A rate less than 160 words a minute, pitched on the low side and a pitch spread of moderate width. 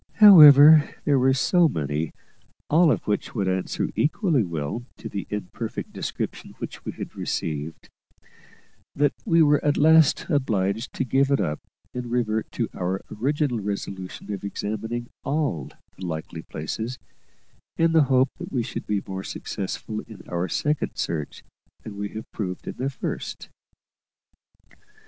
No: average, 150 wpm; low, 115 Hz; wide, 7.0 semitones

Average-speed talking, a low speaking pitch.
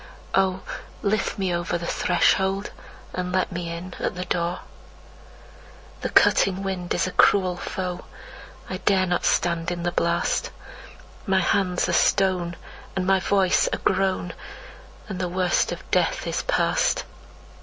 No: average, 145 wpm; medium, 185 Hz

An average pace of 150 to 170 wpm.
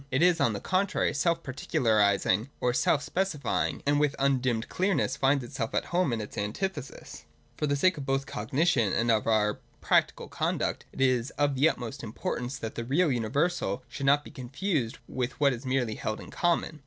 No: average, 190 wpm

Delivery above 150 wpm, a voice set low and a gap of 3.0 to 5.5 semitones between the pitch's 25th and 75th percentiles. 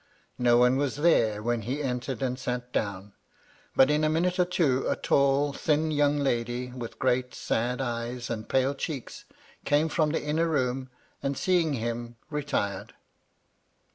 Yes: average, 160 wpm; low, 130 Hz; average, 3.5 semitones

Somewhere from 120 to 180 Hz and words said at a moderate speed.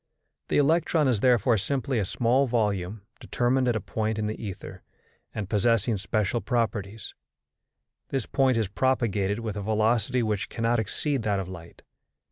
No: low, 110 Hz; average, 155 wpm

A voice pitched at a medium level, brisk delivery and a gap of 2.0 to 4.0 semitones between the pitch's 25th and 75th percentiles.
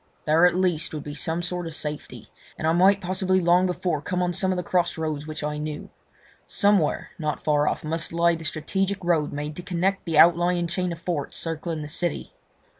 Yes: medium, 170 Hz; fast, 210 wpm; average, 2.7 semitones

